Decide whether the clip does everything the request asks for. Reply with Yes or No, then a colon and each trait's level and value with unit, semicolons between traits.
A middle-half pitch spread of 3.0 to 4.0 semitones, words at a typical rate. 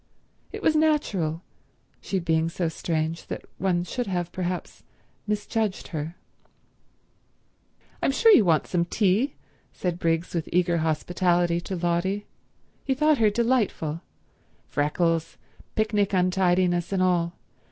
No: average, 3.5 semitones; slow, 120 wpm